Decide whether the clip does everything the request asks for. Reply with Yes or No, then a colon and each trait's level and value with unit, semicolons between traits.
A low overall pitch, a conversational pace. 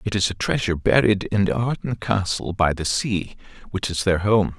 Yes: low, 100 Hz; average, 195 wpm